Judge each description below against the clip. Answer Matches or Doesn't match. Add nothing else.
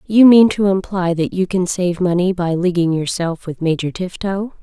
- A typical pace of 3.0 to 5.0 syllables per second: Matches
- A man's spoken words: Doesn't match